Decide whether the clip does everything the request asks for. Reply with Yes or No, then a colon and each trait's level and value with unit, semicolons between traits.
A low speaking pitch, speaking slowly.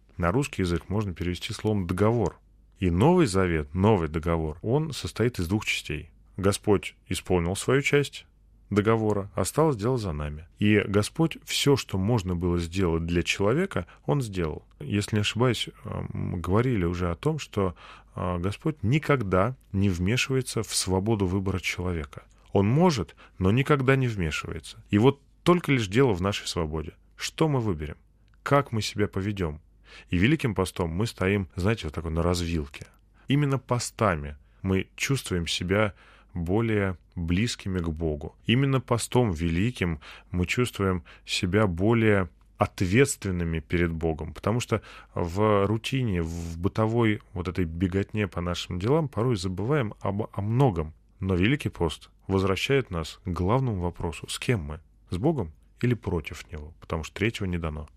No: low, 100 Hz; average, 145 wpm